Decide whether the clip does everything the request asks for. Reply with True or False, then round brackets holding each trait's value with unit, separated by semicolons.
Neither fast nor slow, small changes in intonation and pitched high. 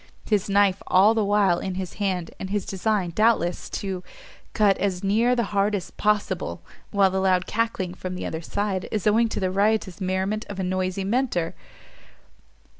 True (180 wpm; 2.2 semitones; 195 Hz)